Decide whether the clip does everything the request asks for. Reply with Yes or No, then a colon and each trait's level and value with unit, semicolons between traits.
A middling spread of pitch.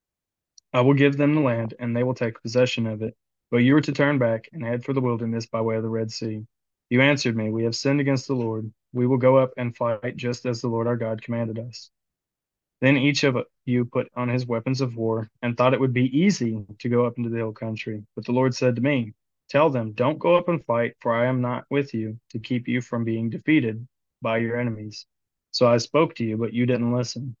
No: narrow, 2.3 semitones